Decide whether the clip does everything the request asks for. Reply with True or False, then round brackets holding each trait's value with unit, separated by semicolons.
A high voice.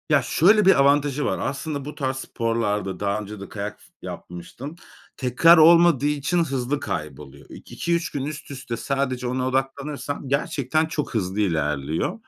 False (135 Hz)